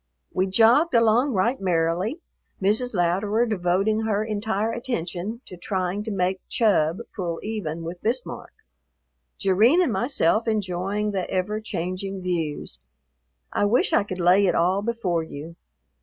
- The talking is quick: No, average, 140 wpm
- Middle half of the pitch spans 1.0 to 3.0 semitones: No, average, 3.7 semitones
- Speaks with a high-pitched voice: Yes, high, 195 Hz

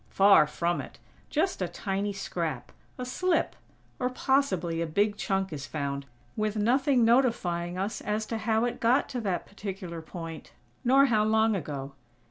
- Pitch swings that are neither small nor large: No, wide, 5.7 semitones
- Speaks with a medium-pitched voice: No, high, 205 Hz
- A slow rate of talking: No, average, 160 wpm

